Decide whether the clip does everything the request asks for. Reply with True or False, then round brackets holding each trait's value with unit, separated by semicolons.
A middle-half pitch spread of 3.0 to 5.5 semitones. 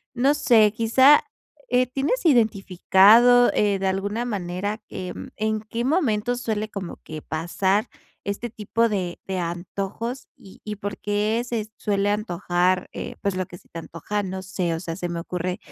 True (3.8 semitones)